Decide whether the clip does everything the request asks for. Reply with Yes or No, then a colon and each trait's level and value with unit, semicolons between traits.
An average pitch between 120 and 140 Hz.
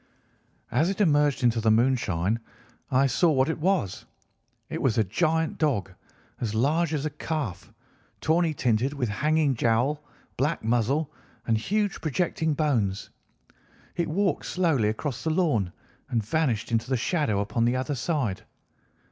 Yes: low, 135 Hz